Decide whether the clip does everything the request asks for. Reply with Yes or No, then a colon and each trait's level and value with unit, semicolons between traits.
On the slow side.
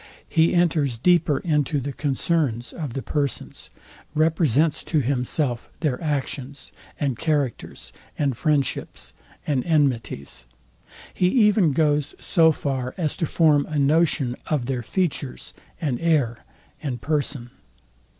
Yes: slow, 120 wpm